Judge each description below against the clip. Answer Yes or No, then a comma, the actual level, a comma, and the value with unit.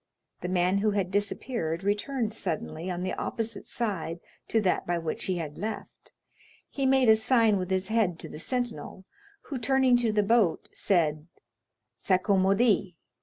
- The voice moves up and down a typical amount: Yes, average, 4.1 semitones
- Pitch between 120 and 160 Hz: No, high, 200 Hz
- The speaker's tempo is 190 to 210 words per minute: No, average, 160 wpm